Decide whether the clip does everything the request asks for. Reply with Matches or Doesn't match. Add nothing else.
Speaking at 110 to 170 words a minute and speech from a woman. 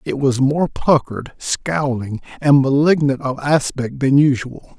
Doesn't match